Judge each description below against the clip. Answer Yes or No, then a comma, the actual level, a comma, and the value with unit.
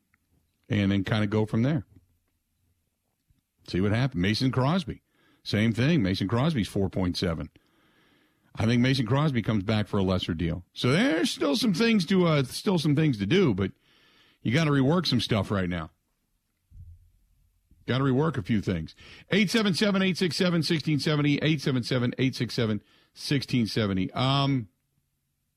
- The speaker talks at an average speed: Yes, average, 165 wpm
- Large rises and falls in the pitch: Yes, wide, 8.1 semitones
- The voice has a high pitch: No, low, 115 Hz